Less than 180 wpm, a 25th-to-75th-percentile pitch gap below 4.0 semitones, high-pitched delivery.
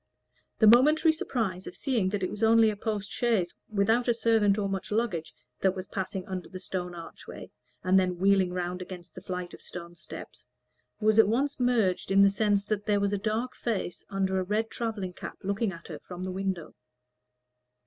No: average, 200 wpm; average, 3.3 semitones; high, 200 Hz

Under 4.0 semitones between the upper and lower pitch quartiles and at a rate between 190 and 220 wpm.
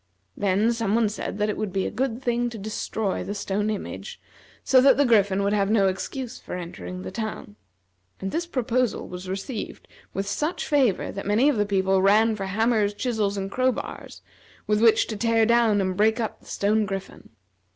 Yes: average, 3.1 semitones; average, 195 wpm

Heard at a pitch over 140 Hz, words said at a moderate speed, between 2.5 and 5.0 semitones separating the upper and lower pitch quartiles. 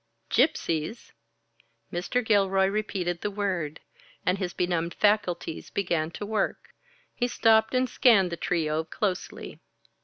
No: high, 190 Hz; slow, 120 wpm; average, 3.8 semitones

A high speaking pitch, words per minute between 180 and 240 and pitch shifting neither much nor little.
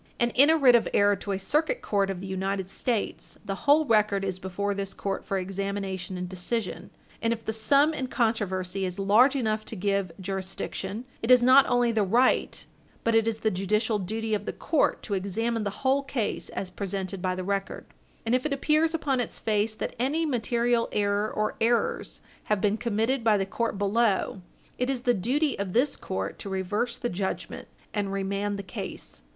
Yes: high, 210 Hz; average, 200 wpm; average, 3.7 semitones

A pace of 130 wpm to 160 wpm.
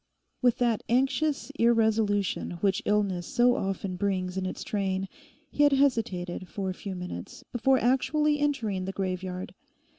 Yes: average, 145 wpm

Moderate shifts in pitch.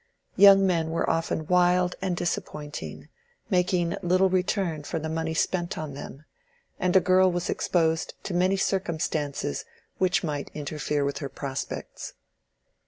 Yes: average, 3.0 semitones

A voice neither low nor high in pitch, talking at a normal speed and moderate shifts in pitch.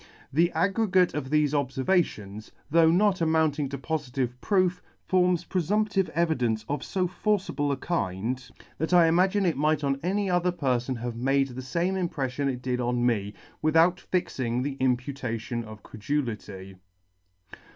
No: medium, 145 Hz; average, 145 wpm; wide, 6.1 semitones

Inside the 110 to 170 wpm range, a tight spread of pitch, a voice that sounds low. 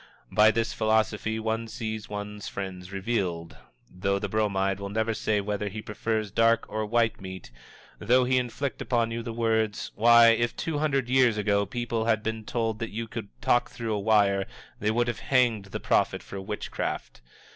No: average, 180 wpm; narrow, 2.2 semitones; low, 110 Hz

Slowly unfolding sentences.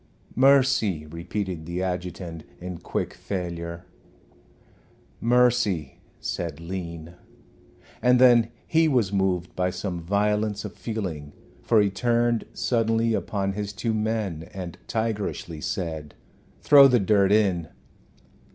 Yes: slow, 115 wpm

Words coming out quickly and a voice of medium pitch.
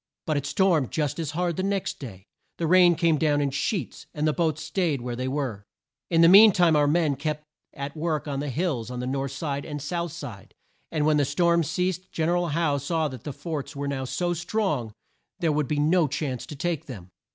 Yes: fast, 230 wpm; medium, 150 Hz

